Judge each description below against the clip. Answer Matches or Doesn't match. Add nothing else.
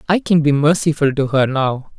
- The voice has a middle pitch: Matches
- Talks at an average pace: Doesn't match